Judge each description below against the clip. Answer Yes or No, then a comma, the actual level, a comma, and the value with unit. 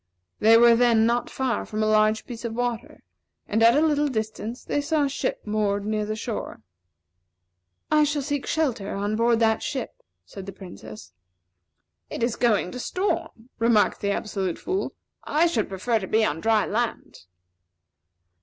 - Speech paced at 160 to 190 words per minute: Yes, average, 170 wpm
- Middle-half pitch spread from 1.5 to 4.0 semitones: Yes, average, 2.9 semitones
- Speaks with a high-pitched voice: Yes, high, 225 Hz